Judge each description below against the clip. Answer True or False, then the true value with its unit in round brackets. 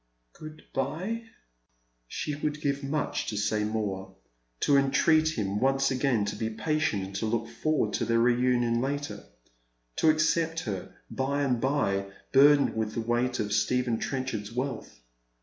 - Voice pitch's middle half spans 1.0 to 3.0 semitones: False (5.3 semitones)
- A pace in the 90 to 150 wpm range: False (160 wpm)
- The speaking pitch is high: False (125 Hz)